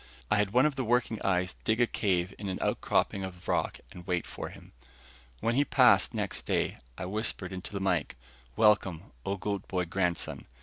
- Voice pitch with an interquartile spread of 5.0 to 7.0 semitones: No, average, 3.2 semitones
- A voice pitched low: Yes, very low, 95 Hz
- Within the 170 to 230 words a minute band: Yes, average, 190 wpm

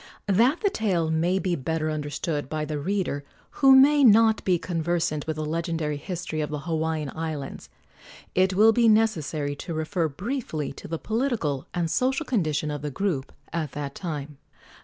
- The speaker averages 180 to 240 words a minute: No, average, 170 wpm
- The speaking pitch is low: No, medium, 165 Hz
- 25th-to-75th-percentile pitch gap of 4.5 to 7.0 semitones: Yes, average, 5.1 semitones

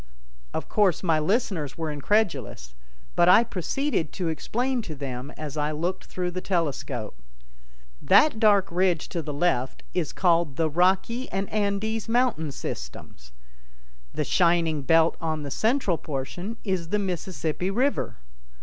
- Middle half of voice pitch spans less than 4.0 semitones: No, average, 4.8 semitones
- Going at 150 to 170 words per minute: No, average, 140 wpm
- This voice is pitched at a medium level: Yes, medium, 175 Hz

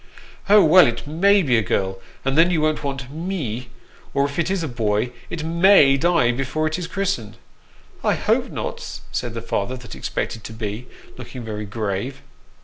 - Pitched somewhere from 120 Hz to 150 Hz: Yes, low, 135 Hz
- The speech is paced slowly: No, average, 190 wpm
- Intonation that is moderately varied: No, wide, 6.5 semitones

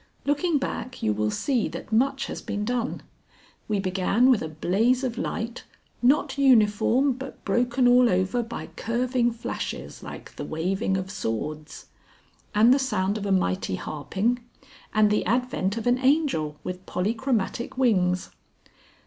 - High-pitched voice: Yes, high, 230 Hz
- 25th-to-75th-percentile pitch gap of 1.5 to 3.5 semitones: No, average, 5.1 semitones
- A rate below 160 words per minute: Yes, average, 150 wpm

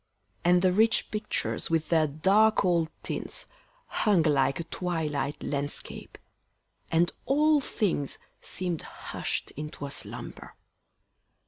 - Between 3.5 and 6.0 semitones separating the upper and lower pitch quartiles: Yes, average, 4.7 semitones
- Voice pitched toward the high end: No, medium, 170 Hz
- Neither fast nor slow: No, slow, 115 wpm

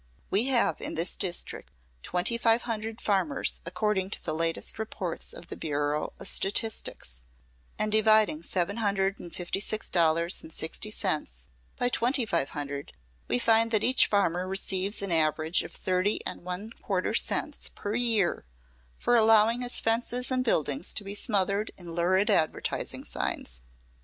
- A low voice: No, high, 195 Hz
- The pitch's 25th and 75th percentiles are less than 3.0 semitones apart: No, average, 4.7 semitones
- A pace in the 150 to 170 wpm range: Yes, average, 155 wpm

